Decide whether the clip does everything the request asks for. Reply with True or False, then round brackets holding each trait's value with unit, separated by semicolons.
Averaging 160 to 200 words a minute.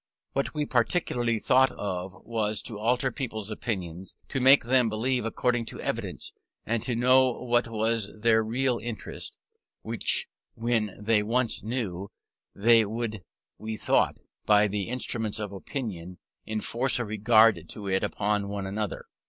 False (145 wpm)